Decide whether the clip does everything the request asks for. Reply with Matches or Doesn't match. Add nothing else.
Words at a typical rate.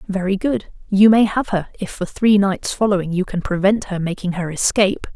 Doesn't match